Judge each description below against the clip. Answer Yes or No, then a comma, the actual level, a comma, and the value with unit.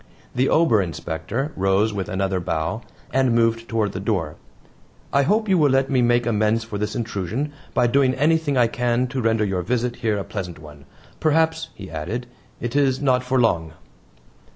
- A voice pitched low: Yes, low, 115 Hz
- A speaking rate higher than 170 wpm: Yes, average, 180 wpm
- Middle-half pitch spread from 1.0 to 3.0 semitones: No, average, 5.2 semitones